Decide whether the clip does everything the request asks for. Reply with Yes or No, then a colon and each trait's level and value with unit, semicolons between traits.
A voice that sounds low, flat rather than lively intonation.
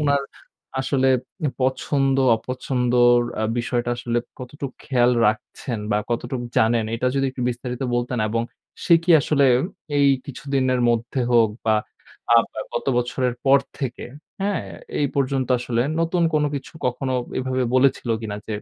Yes: low, 125 Hz; narrow, 2.2 semitones